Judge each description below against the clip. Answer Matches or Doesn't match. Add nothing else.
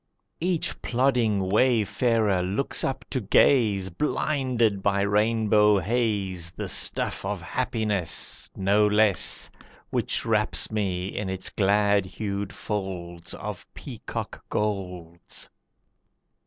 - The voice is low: Matches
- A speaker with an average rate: Doesn't match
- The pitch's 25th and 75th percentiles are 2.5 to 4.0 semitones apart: Matches